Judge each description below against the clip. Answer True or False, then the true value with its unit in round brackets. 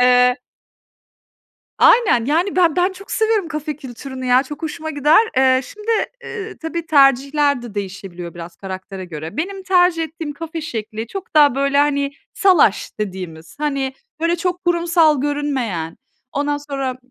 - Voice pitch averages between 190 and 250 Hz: False (285 Hz)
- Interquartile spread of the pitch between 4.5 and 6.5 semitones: True (5.3 semitones)